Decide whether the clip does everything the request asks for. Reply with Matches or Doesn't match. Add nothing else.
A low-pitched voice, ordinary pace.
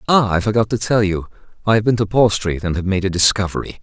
Doesn't match